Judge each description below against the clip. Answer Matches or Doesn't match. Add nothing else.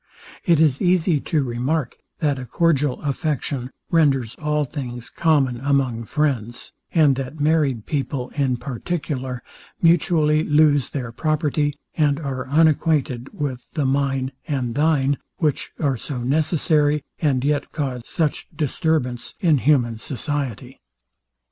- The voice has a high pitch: Doesn't match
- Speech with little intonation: Doesn't match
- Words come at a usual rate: Doesn't match